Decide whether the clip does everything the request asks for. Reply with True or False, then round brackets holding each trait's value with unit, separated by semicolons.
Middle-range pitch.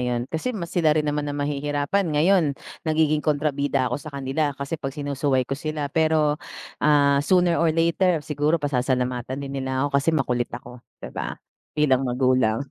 True (145 Hz)